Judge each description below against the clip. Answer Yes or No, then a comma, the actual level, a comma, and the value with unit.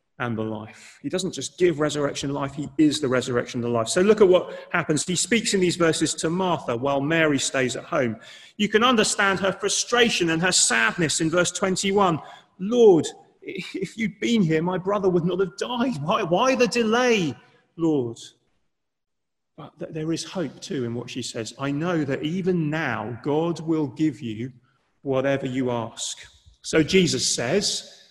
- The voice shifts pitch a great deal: Yes, wide, 6.0 semitones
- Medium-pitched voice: Yes, medium, 165 Hz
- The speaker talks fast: No, average, 175 wpm